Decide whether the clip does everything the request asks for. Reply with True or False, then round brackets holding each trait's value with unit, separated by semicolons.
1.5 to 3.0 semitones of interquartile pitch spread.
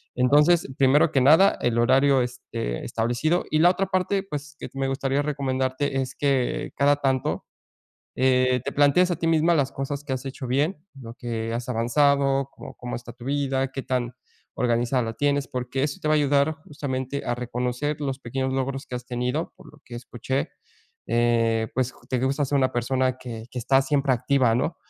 True (2.6 semitones)